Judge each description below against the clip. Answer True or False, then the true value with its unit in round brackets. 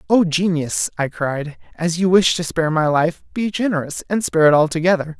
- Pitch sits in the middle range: True (165 Hz)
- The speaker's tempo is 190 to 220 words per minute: True (195 wpm)